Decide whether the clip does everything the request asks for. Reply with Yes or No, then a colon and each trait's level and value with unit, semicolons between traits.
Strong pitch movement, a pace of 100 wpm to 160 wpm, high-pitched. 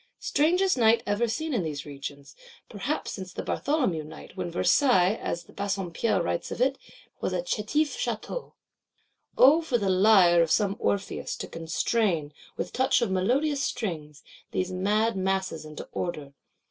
Yes: wide, 6.7 semitones; average, 145 wpm; high, 200 Hz